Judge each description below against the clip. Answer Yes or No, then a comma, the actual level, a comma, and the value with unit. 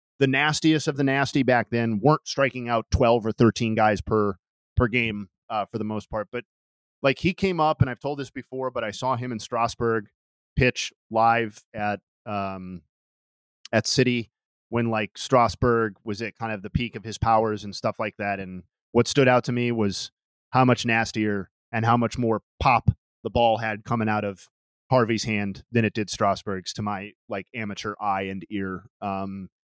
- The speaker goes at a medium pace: Yes, average, 190 wpm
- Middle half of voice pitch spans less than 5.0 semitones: Yes, average, 3.2 semitones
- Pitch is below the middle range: Yes, low, 110 Hz